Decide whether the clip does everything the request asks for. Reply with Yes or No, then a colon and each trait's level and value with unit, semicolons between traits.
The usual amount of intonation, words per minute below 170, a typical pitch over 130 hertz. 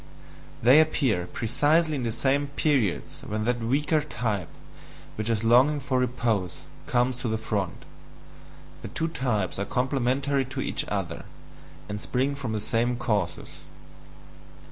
No: average, 4.2 semitones; average, 140 wpm; low, 125 Hz